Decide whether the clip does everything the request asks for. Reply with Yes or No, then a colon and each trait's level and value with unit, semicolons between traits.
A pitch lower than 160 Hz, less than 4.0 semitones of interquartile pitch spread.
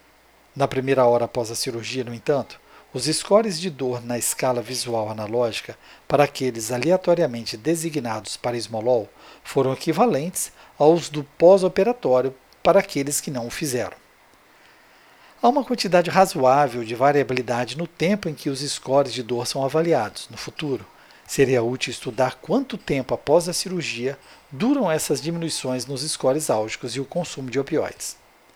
No: medium, 140 Hz; average, 4.9 semitones